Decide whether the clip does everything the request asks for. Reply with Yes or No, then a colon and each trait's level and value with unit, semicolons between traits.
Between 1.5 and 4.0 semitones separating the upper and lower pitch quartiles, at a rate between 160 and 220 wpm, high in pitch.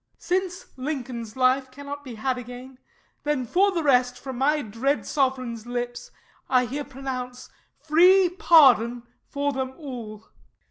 No: average, 2.8 semitones; average, 140 wpm; very high, 260 Hz